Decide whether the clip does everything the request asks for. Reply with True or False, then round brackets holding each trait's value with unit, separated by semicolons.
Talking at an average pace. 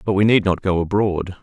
False (255 wpm)